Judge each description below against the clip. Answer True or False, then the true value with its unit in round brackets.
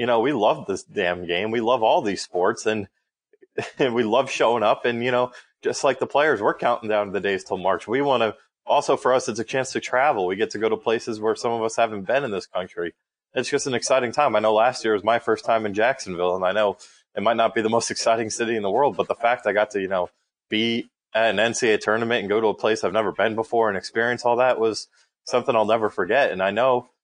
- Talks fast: True (270 wpm)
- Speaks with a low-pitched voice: True (115 Hz)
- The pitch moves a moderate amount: False (1.9 semitones)